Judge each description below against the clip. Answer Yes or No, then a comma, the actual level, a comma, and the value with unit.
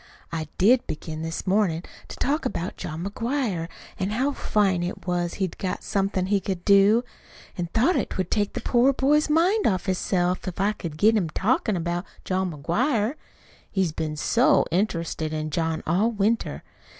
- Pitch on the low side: No, high, 190 Hz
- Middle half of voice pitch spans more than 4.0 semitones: Yes, average, 4.6 semitones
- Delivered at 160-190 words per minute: Yes, average, 170 wpm